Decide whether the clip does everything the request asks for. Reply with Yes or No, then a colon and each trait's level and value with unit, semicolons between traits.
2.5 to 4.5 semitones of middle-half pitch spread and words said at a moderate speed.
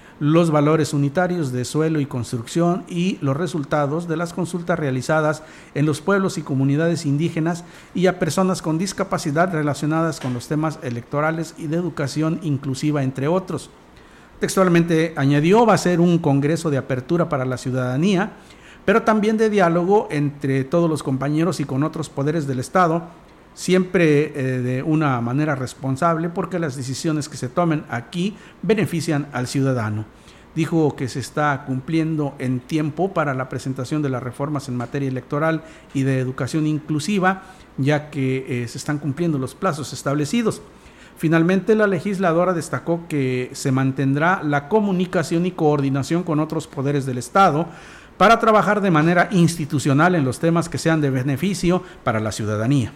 Yes: average, 3.9 semitones; average, 155 wpm